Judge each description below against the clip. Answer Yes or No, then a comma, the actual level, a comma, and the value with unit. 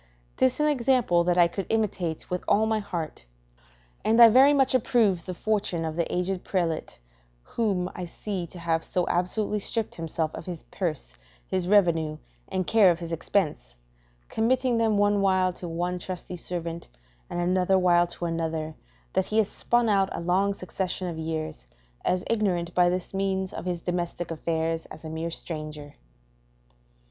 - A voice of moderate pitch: Yes, medium, 180 Hz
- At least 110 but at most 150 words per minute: No, average, 170 wpm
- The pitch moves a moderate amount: Yes, average, 3.3 semitones